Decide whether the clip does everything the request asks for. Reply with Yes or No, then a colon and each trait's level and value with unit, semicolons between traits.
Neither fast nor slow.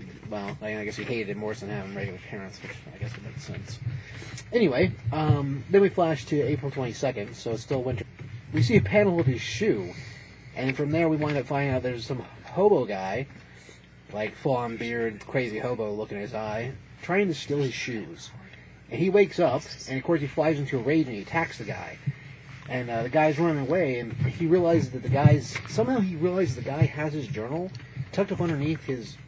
No: fast, 210 wpm